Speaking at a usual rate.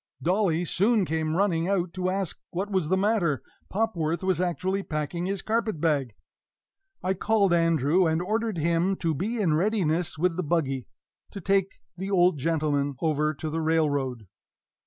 Yes: average, 160 wpm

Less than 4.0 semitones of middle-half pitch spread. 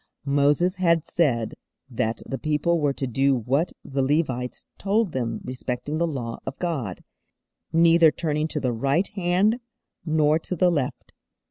No: average, 4.3 semitones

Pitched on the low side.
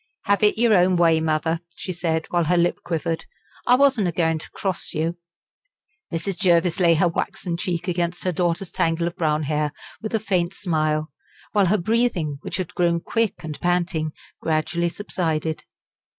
No: medium, 170 Hz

